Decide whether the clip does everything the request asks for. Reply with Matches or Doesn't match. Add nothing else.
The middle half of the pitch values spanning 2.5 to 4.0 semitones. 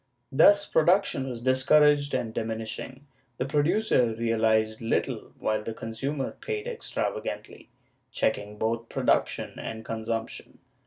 Doesn't match